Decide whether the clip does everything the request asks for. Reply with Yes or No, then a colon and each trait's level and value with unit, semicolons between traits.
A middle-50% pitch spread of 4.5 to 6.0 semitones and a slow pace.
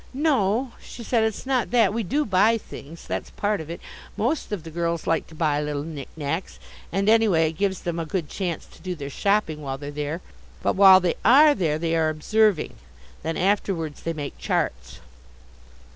No: average, 5.0 semitones; average, 195 wpm